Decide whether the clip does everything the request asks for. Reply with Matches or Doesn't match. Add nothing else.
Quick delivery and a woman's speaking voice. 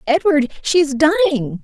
Doesn't match